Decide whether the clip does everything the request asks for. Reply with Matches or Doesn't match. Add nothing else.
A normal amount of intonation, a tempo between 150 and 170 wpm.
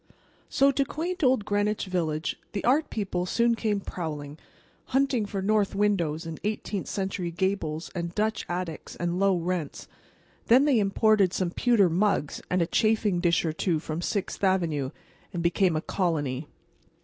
Matches